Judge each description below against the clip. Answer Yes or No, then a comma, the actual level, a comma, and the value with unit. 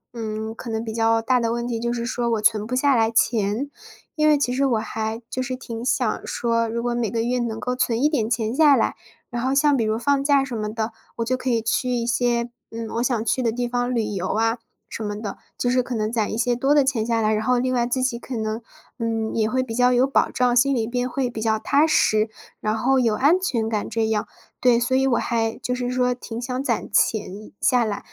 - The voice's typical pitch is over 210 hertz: Yes, high, 235 Hz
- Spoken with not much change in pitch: Yes, narrow, 2.2 semitones